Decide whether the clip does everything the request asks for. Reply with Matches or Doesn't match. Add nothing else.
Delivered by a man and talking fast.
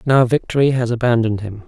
Doesn't match